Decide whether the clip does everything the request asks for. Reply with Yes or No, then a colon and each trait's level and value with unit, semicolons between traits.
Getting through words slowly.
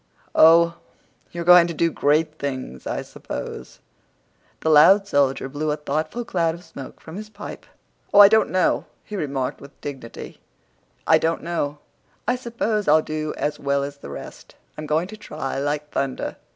No: average, 170 wpm